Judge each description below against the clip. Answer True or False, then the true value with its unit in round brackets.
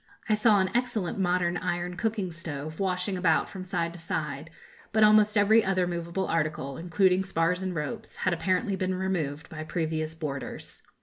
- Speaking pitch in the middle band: True (180 Hz)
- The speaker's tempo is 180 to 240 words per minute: False (170 wpm)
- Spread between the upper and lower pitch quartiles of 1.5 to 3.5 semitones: True (2.8 semitones)